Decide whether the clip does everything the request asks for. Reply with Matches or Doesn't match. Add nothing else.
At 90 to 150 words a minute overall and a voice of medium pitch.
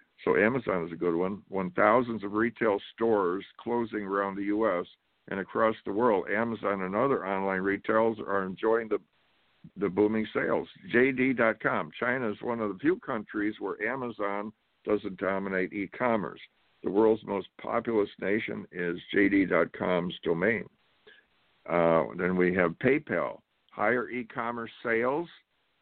Doesn't match